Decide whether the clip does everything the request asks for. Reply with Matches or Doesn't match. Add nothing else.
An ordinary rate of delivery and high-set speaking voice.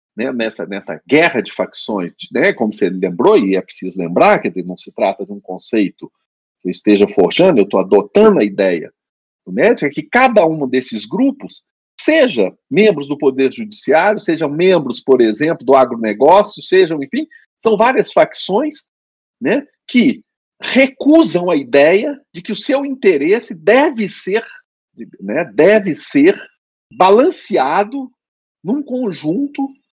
Matches